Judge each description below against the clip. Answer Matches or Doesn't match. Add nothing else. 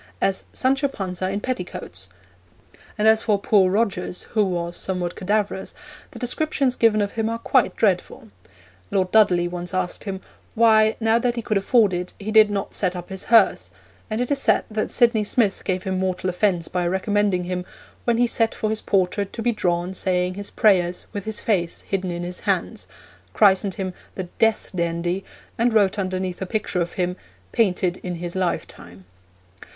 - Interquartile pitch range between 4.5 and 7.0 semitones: Doesn't match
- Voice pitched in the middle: Doesn't match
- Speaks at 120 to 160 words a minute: Doesn't match